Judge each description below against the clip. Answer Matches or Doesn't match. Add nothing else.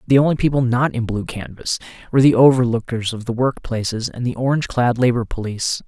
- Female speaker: Doesn't match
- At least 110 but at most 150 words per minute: Doesn't match